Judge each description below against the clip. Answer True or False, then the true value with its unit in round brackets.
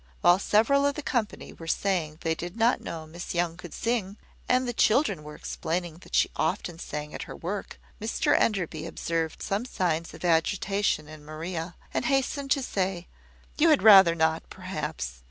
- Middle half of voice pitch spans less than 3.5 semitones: False (5.1 semitones)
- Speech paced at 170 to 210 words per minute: True (175 wpm)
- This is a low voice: False (175 Hz)